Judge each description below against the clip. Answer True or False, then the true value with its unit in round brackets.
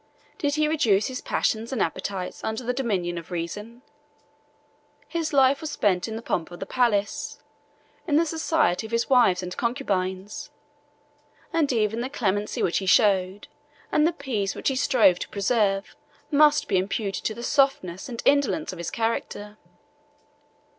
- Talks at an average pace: True (160 wpm)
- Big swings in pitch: True (5.9 semitones)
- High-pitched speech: True (225 Hz)